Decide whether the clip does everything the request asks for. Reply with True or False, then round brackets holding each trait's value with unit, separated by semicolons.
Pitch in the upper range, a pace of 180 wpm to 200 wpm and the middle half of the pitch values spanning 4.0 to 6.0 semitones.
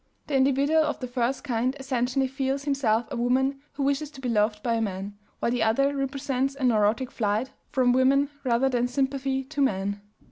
False (260 Hz; 190 wpm; 2.6 semitones)